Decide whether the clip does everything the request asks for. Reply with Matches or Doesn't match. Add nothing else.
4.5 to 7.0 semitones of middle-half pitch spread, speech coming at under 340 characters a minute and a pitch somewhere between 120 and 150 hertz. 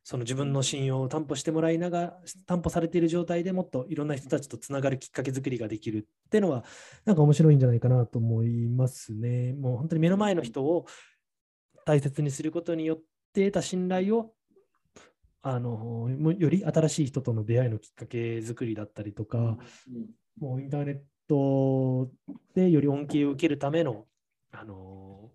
Doesn't match